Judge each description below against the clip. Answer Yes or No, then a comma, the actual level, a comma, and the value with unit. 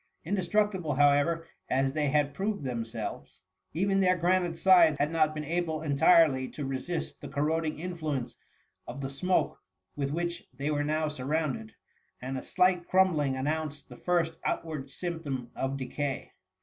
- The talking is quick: No, average, 160 wpm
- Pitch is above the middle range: No, medium, 155 Hz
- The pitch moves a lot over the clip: No, average, 3.8 semitones